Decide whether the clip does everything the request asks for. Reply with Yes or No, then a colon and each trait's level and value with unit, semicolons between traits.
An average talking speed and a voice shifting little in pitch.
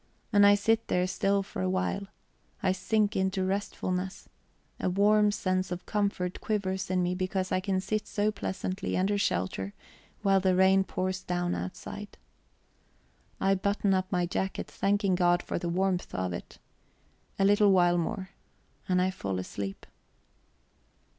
Yes: average, 155 wpm; narrow, 1.7 semitones